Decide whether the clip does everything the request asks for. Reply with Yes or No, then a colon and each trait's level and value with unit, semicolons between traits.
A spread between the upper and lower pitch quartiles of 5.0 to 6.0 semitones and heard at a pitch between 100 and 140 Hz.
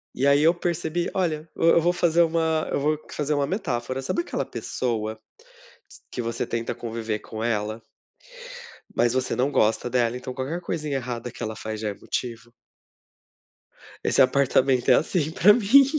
Yes: wide, 5.5 semitones; low, 135 Hz